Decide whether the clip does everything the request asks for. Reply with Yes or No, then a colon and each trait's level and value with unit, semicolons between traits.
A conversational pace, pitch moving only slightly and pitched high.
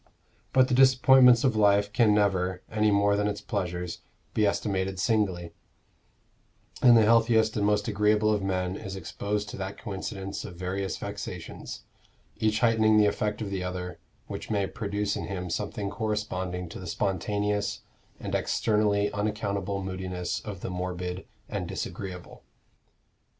No: average, 145 wpm; narrow, 2.3 semitones; low, 100 Hz